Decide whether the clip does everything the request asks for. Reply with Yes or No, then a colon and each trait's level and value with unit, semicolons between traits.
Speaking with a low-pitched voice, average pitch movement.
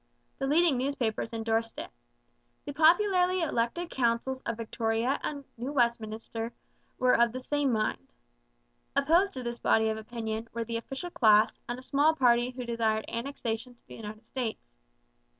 No: high, 240 Hz; average, 3.6 semitones